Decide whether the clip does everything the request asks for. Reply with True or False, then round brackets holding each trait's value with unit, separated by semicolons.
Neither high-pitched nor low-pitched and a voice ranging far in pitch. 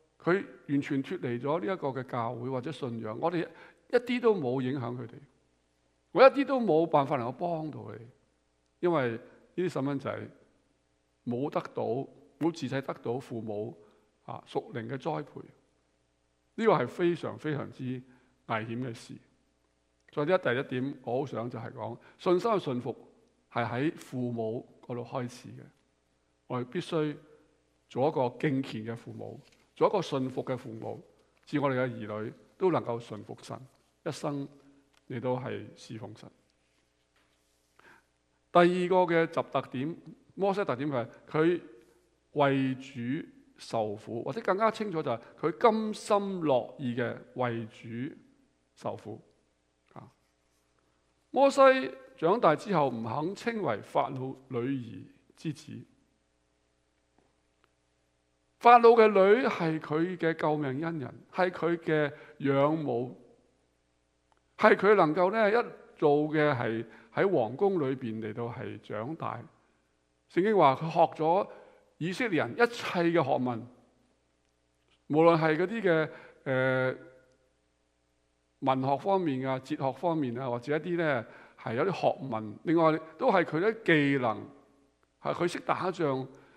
False (130 Hz; 6.8 semitones)